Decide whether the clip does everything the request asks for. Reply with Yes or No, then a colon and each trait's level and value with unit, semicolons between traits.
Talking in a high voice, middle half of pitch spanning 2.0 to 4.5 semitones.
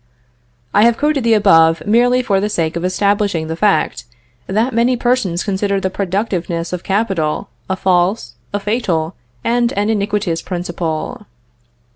Yes: high, 200 Hz; average, 4.2 semitones